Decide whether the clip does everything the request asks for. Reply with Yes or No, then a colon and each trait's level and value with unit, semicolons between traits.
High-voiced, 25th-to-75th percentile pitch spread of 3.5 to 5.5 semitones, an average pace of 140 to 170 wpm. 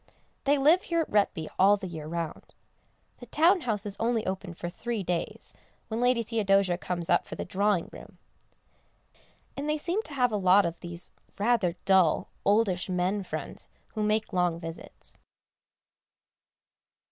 Yes: high, 200 Hz; average, 4.9 semitones; average, 160 wpm